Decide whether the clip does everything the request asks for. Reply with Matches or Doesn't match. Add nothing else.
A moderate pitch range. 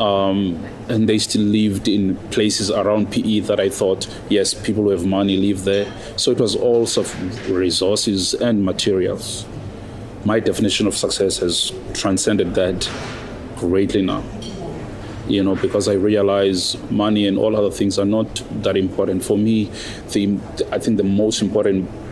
Doesn't match